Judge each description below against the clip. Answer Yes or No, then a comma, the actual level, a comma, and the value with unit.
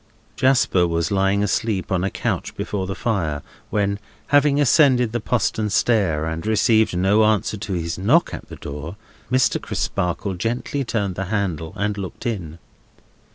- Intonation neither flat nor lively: Yes, average, 4.0 semitones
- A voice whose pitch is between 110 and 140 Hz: No, low, 100 Hz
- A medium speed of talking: Yes, average, 155 wpm